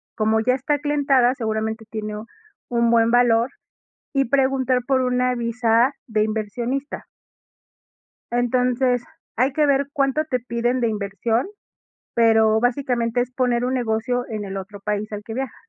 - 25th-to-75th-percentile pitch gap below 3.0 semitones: Yes, narrow, 2.6 semitones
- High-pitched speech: Yes, high, 240 Hz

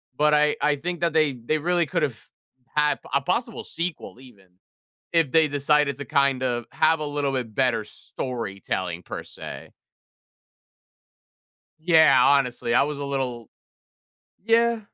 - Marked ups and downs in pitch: No, average, 3.9 semitones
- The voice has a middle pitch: Yes, medium, 145 Hz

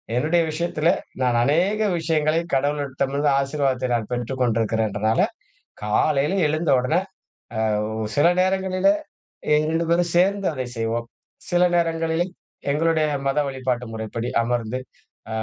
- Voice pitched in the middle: Yes, medium, 145 Hz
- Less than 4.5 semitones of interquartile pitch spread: No, average, 5.2 semitones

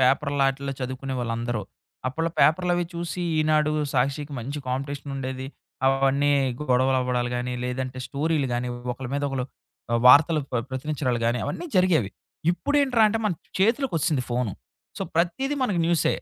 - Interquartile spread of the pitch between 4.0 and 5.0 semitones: Yes, average, 4.4 semitones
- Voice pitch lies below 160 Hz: Yes, medium, 140 Hz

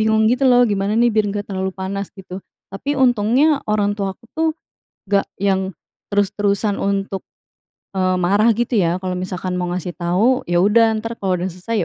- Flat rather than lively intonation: No, average, 3.2 semitones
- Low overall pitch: No, high, 200 Hz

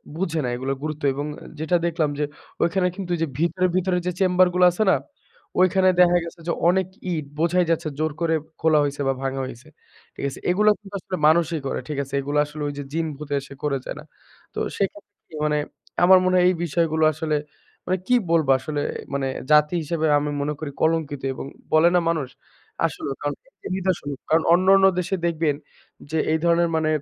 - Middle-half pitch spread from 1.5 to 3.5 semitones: Yes, average, 3.2 semitones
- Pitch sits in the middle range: Yes, medium, 160 Hz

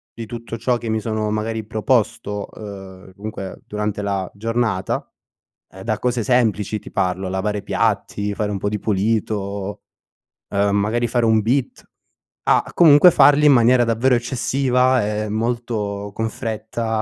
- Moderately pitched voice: No, low, 110 Hz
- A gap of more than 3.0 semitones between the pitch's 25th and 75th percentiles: No, narrow, 2.6 semitones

